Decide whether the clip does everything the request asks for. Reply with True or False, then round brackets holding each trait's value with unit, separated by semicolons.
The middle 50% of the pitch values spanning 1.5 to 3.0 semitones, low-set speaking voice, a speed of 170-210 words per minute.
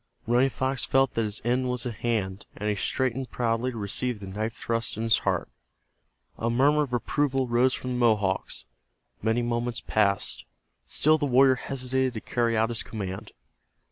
True (2.7 semitones; 120 Hz; 175 wpm)